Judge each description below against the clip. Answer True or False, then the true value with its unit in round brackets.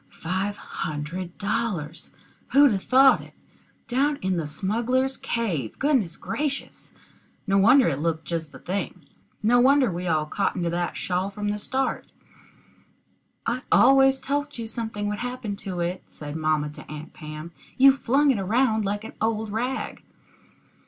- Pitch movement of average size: False (6.8 semitones)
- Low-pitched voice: False (205 Hz)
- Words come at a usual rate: True (155 wpm)